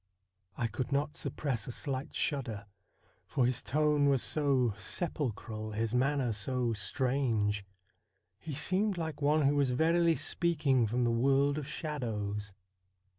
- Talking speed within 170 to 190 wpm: No, slow, 135 wpm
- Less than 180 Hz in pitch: Yes, low, 135 Hz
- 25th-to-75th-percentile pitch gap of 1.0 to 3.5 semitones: No, average, 4.4 semitones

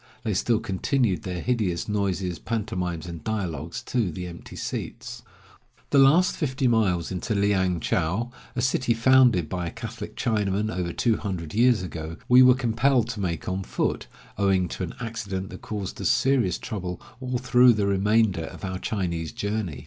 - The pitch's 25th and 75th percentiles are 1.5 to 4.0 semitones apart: No, average, 4.7 semitones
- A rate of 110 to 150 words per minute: No, average, 170 wpm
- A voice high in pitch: No, low, 100 Hz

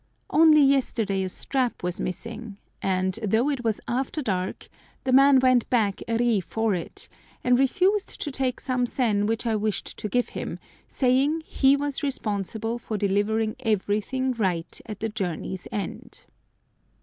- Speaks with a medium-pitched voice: No, high, 225 Hz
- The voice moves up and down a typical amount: Yes, average, 4.3 semitones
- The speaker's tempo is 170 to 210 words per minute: No, average, 155 wpm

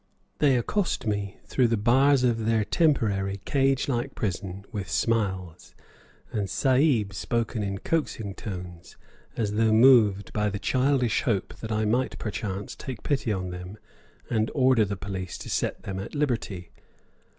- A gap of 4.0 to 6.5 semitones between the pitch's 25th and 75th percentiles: Yes, average, 4.4 semitones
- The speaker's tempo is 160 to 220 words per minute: No, average, 150 wpm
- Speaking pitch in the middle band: No, low, 110 Hz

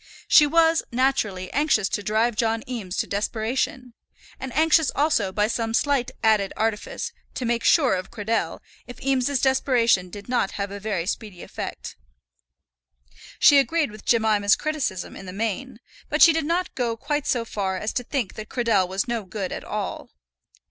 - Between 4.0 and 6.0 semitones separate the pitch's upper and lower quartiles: Yes, average, 4.6 semitones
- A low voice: No, high, 230 Hz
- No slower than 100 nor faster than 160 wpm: No, average, 170 wpm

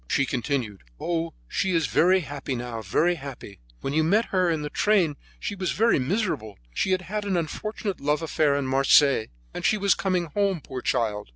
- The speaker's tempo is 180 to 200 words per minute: Yes, average, 195 wpm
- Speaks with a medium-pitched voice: Yes, medium, 160 Hz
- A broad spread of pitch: Yes, wide, 5.8 semitones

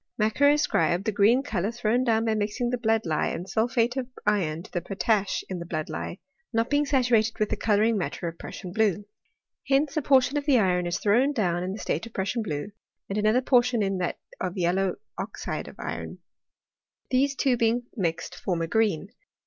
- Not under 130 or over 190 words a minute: No, fast, 205 wpm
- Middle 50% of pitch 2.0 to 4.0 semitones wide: No, average, 4.7 semitones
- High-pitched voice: Yes, high, 215 Hz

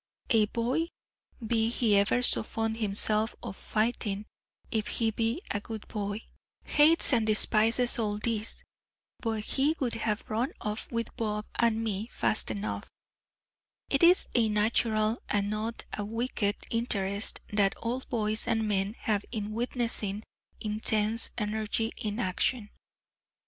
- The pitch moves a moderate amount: No, narrow, 1.8 semitones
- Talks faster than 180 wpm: No, average, 140 wpm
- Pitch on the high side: Yes, high, 220 Hz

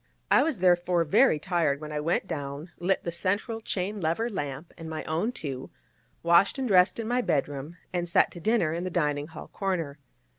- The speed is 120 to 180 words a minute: No, average, 195 wpm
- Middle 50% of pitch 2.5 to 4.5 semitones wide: Yes, average, 3.9 semitones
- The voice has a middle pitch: Yes, medium, 170 Hz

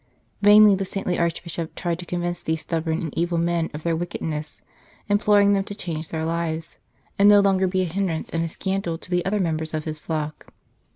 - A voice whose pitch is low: No, medium, 170 Hz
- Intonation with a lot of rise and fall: No, average, 3.0 semitones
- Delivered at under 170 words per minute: No, fast, 205 wpm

